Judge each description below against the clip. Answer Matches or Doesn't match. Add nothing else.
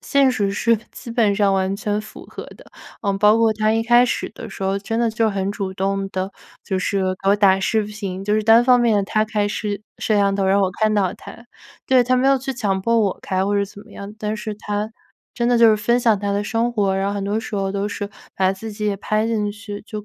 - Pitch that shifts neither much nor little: Doesn't match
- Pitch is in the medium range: Doesn't match